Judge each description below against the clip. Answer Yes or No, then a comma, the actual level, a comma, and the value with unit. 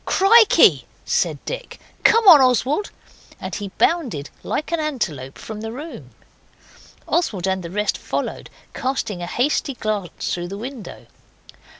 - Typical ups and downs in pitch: No, wide, 8.3 semitones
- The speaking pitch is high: Yes, high, 245 Hz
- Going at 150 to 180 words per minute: No, slow, 135 wpm